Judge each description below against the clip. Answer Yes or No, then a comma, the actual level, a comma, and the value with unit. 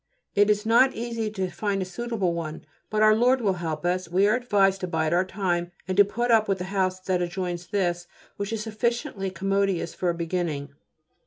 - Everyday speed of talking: No, fast, 210 wpm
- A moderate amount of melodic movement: Yes, average, 3.4 semitones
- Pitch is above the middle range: Yes, high, 195 Hz